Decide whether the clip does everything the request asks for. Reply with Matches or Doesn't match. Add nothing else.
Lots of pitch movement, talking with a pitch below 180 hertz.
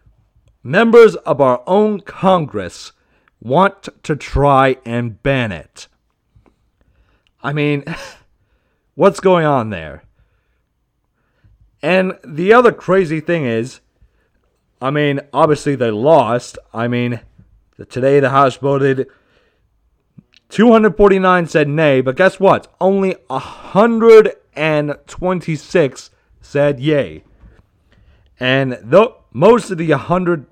Matches